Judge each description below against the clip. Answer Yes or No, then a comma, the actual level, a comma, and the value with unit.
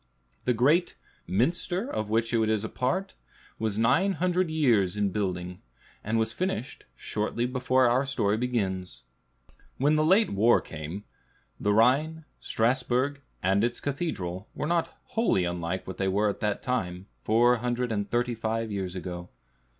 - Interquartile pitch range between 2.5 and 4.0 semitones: No, average, 5.1 semitones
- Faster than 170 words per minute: No, average, 155 wpm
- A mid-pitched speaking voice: No, low, 115 Hz